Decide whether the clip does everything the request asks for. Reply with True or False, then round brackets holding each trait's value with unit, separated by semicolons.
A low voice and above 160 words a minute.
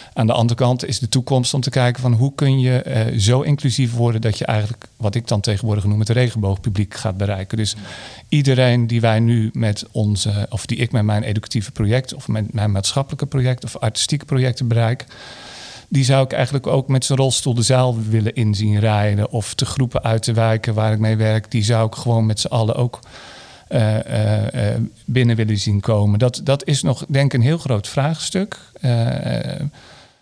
True (115 Hz; 200 wpm)